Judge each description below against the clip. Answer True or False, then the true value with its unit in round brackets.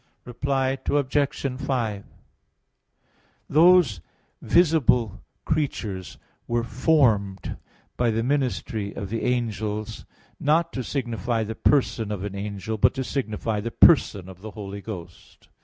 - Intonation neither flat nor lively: True (4.7 semitones)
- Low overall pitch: True (115 Hz)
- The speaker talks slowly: True (120 wpm)